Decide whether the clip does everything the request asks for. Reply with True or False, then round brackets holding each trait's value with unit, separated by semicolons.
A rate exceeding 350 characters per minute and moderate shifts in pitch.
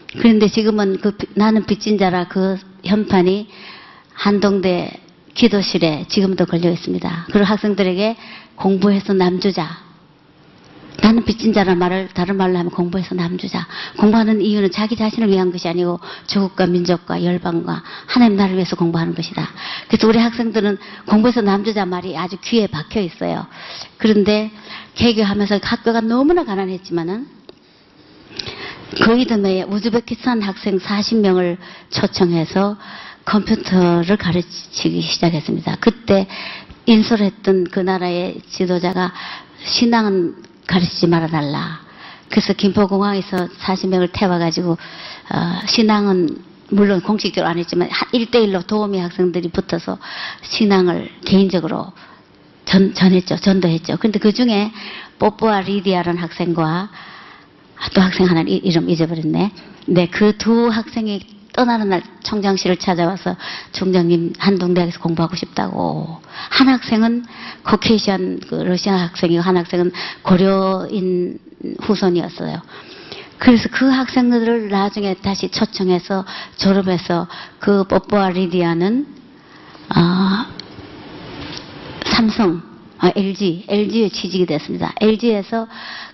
False (290 characters per minute; 3.2 semitones)